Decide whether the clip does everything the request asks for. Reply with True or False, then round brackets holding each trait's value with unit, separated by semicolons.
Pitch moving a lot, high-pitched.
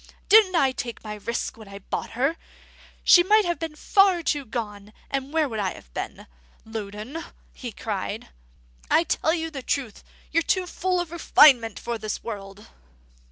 True (7.5 semitones; 260 Hz)